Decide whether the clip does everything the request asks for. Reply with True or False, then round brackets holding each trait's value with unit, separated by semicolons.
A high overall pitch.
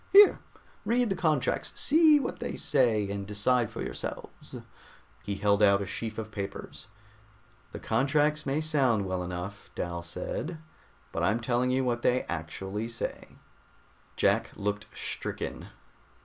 False (115 Hz)